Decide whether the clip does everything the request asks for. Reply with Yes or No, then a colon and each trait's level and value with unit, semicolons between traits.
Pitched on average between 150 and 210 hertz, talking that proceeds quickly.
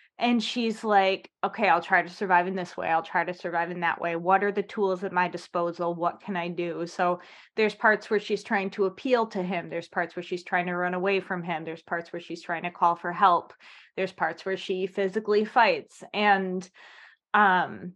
Yes: medium, 185 Hz; fast, 220 wpm